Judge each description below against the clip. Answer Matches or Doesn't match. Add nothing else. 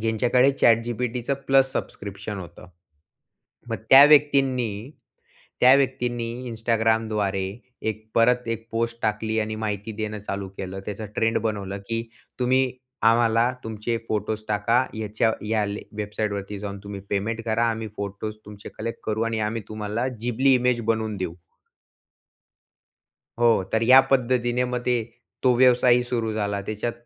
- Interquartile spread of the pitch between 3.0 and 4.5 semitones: Doesn't match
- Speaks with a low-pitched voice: Matches